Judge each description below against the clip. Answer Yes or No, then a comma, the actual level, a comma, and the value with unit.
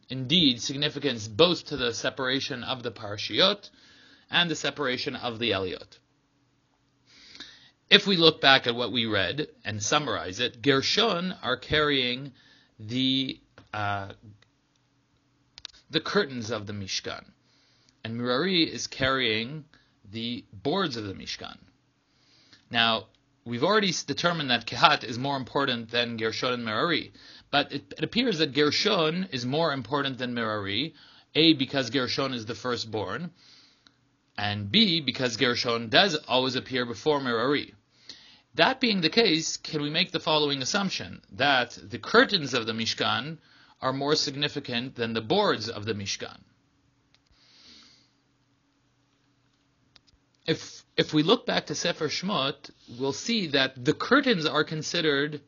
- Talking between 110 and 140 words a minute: Yes, slow, 135 wpm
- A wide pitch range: No, average, 4.0 semitones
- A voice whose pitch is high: No, low, 135 Hz